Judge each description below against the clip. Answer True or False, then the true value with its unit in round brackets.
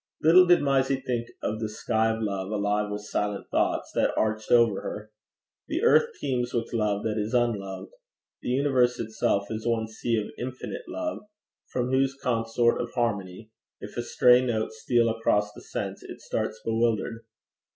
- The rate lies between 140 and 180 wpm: True (170 wpm)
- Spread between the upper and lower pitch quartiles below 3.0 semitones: True (2.6 semitones)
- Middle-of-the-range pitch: False (115 Hz)